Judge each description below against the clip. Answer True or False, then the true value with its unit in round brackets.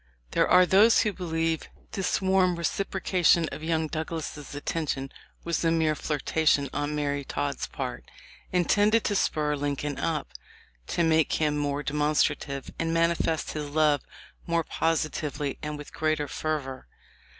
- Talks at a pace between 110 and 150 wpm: True (140 wpm)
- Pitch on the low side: False (155 Hz)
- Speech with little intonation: True (2.3 semitones)